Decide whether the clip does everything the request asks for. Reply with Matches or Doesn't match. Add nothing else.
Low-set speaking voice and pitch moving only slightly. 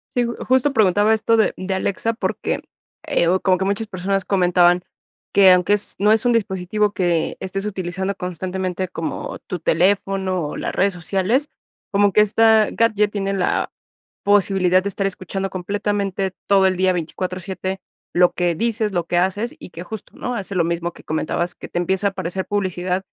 Doesn't match